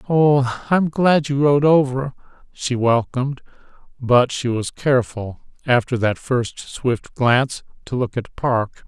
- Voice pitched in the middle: No, low, 130 Hz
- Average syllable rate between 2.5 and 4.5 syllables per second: Yes, 3.9 syllables/s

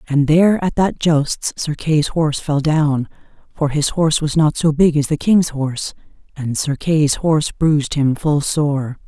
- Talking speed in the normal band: Yes, average, 190 wpm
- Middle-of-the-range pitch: Yes, medium, 150 Hz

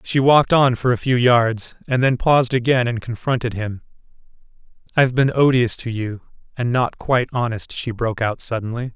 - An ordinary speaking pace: Yes, average, 175 wpm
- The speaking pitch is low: Yes, low, 120 Hz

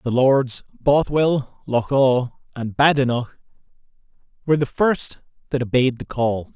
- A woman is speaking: No, male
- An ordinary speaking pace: No, slow, 130 wpm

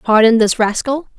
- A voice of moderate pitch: No, high, 235 Hz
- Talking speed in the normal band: Yes, average, 150 wpm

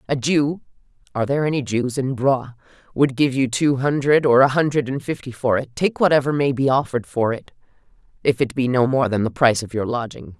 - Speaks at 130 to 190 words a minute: No, average, 200 wpm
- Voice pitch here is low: Yes, low, 130 Hz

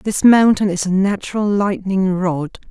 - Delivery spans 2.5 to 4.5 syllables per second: Yes, 4.3 syllables/s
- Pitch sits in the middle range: No, high, 195 Hz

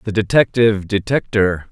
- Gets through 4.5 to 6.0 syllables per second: Yes, 5.1 syllables/s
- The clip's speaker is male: Yes, male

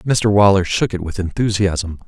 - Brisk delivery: No, average, 175 wpm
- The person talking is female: No, male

